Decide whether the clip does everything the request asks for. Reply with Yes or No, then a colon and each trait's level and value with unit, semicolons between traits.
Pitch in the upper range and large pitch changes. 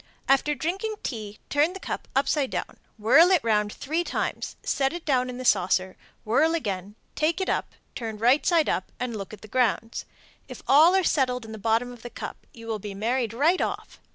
Yes: very high, 250 Hz; wide, 5.8 semitones